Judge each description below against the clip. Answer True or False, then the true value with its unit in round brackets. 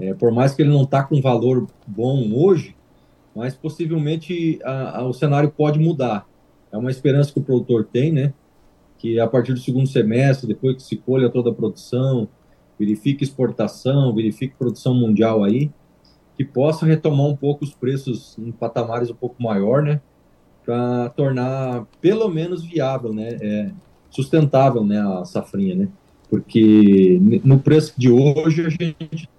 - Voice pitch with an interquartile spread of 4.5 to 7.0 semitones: False (4.0 semitones)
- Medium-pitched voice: False (130 Hz)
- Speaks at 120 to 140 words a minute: False (160 wpm)